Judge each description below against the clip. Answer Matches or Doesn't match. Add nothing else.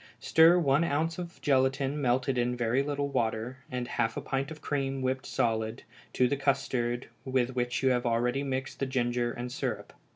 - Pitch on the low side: Matches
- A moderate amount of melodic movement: Doesn't match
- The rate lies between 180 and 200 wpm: Matches